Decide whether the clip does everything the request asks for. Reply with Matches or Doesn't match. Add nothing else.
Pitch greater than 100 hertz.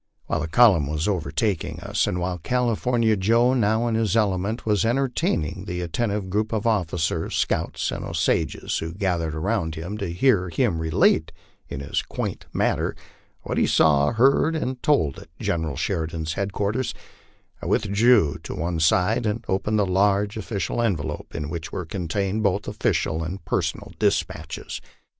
Doesn't match